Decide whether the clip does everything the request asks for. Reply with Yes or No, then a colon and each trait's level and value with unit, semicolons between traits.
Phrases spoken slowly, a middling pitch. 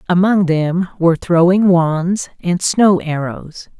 Yes: slow, 125 wpm; medium, 175 Hz